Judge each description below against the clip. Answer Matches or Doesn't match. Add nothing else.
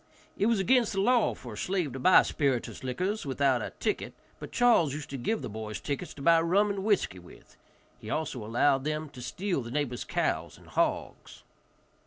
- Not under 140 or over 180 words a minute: Doesn't match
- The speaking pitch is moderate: Matches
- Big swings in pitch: Matches